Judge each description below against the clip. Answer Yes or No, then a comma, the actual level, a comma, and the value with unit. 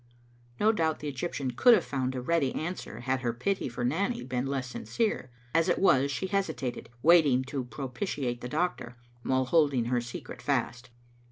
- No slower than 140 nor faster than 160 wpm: No, average, 180 wpm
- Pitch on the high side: No, low, 135 Hz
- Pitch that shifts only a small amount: No, average, 5.1 semitones